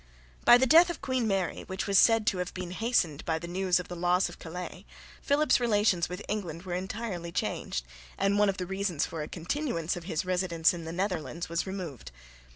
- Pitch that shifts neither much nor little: Yes, average, 3.3 semitones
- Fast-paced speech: Yes, fast, 210 wpm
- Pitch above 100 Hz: Yes, medium, 185 Hz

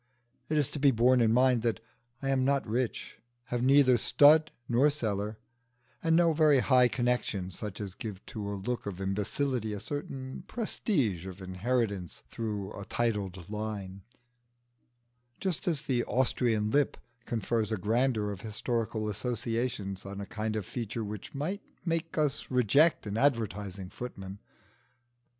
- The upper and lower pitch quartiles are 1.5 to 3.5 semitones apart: No, average, 4.4 semitones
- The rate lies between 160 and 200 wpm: No, average, 150 wpm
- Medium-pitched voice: No, low, 115 Hz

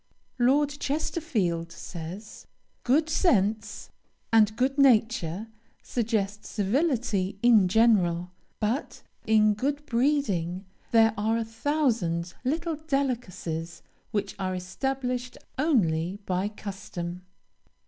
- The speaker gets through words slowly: Yes, slow, 95 wpm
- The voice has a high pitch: Yes, high, 220 Hz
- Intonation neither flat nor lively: No, wide, 6.2 semitones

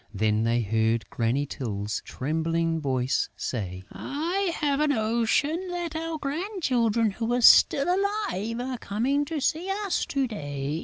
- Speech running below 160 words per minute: Yes, average, 145 wpm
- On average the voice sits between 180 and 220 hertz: No, high, 230 Hz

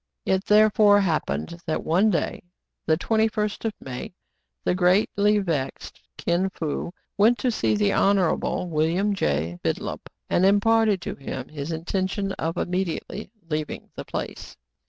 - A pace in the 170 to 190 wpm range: No, slow, 135 wpm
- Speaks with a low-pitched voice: No, medium, 185 Hz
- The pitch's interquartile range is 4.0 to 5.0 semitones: Yes, average, 4.6 semitones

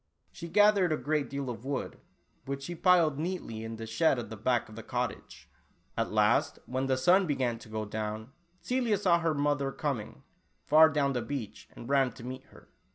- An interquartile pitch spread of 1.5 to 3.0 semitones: No, average, 5.2 semitones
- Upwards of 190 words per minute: Yes, average, 200 wpm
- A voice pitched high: No, medium, 140 Hz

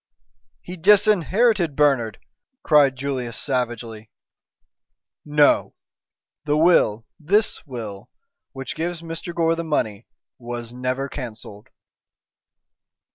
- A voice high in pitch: No, medium, 140 Hz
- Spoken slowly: Yes, slow, 90 wpm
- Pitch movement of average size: No, wide, 5.8 semitones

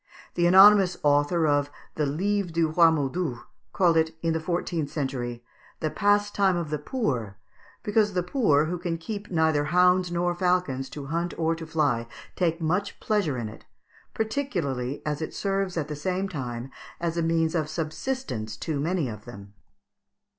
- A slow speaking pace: No, average, 170 wpm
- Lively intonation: No, average, 3.9 semitones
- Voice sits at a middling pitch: Yes, medium, 165 Hz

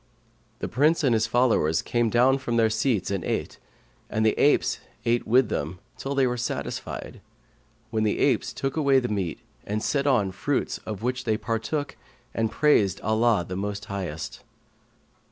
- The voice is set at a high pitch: No, low, 115 Hz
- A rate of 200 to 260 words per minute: No, average, 170 wpm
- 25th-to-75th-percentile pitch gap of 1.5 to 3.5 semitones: No, average, 4.2 semitones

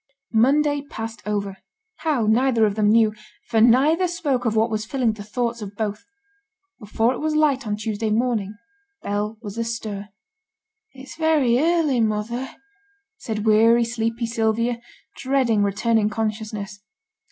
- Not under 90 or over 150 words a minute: Yes, average, 140 wpm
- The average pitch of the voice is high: Yes, high, 230 Hz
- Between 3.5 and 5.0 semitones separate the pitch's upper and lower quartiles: No, average, 3.1 semitones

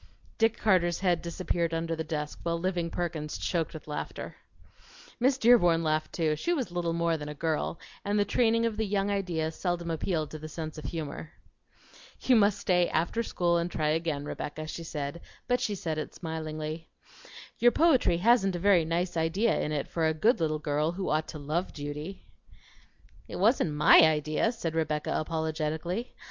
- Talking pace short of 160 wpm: No, average, 180 wpm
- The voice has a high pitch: No, medium, 165 Hz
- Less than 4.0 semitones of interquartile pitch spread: Yes, average, 3.4 semitones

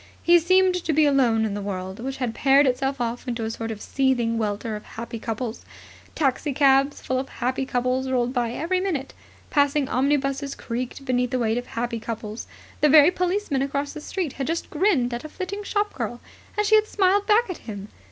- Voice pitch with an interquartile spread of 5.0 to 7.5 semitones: No, average, 4.4 semitones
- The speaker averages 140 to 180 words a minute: No, average, 200 wpm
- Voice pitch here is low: No, very high, 265 Hz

